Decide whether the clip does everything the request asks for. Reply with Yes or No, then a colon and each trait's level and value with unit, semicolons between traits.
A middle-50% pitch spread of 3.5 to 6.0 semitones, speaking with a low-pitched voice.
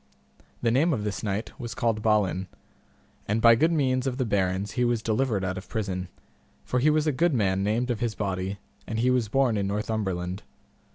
Yes: average, 4.2 semitones; low, 110 Hz